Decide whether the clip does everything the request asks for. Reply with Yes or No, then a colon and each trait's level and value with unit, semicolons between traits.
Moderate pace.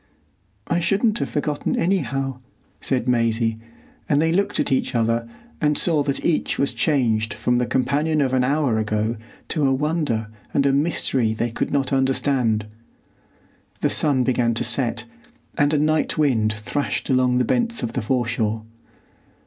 Yes: average, 160 wpm